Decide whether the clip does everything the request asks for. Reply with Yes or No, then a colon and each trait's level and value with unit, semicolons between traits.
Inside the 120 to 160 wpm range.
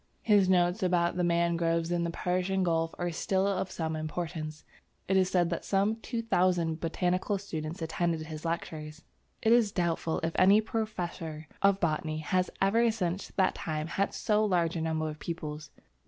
No: average, 170 wpm